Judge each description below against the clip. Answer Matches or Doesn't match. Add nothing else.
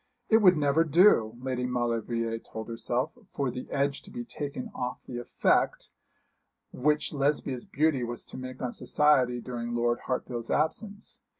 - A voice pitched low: Matches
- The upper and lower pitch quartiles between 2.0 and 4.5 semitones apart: Matches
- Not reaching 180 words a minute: Matches